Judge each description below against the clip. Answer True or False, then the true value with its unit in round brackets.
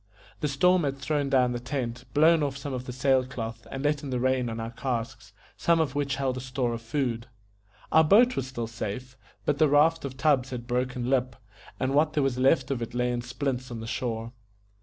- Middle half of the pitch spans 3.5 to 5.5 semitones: False (2.6 semitones)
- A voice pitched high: False (130 Hz)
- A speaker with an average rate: False (225 wpm)